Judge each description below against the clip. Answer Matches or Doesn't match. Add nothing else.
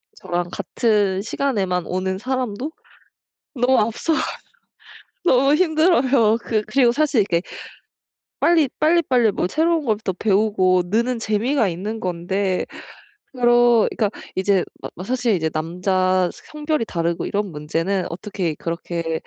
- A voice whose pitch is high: Matches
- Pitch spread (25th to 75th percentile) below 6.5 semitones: Matches